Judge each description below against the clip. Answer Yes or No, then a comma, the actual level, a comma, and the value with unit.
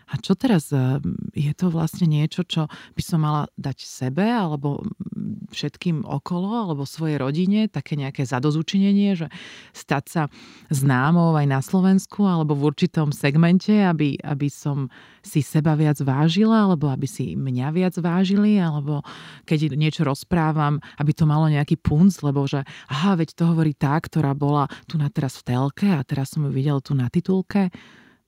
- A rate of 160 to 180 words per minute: Yes, fast, 165 wpm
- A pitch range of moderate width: Yes, average, 4.2 semitones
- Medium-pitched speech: Yes, medium, 155 Hz